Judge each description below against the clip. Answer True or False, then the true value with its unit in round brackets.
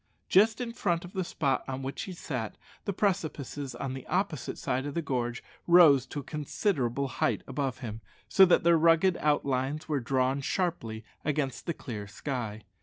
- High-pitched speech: False (140 Hz)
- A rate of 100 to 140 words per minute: False (180 wpm)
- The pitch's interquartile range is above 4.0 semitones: True (4.8 semitones)